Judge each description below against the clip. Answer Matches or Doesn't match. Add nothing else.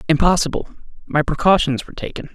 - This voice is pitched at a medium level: Matches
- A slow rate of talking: Matches